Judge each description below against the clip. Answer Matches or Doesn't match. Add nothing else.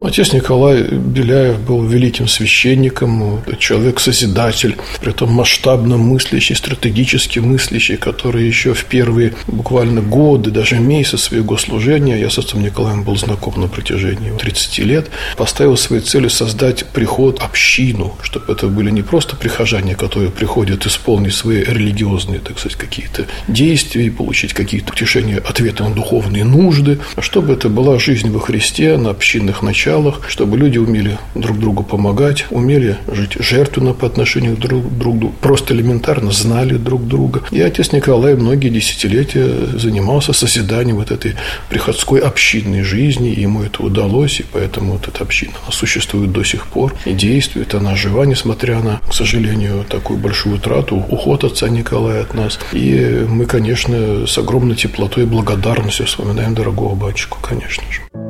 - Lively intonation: Doesn't match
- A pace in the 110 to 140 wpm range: Doesn't match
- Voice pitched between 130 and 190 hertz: Doesn't match